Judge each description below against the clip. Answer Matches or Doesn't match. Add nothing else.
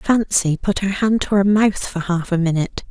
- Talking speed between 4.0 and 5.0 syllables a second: Matches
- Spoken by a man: Doesn't match